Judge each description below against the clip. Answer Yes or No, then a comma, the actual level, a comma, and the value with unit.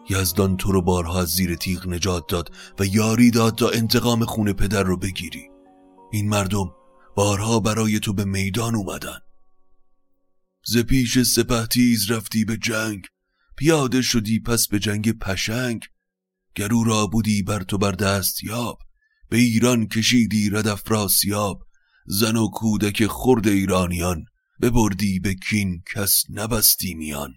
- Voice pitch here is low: Yes, low, 105 Hz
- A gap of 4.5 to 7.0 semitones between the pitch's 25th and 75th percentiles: No, average, 3.3 semitones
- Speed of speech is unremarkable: Yes, average, 135 wpm